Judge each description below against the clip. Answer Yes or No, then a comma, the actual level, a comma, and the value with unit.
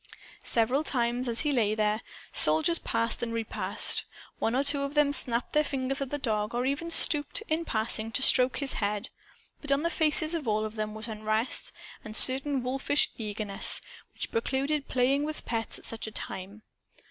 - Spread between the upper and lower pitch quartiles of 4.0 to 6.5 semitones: Yes, average, 4.5 semitones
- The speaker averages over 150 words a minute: Yes, average, 190 wpm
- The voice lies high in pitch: Yes, very high, 250 Hz